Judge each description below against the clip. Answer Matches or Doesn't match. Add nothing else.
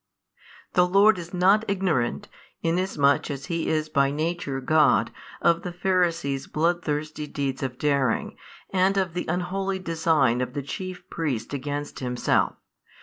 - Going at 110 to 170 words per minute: Matches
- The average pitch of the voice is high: Doesn't match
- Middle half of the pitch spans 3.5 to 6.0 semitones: Matches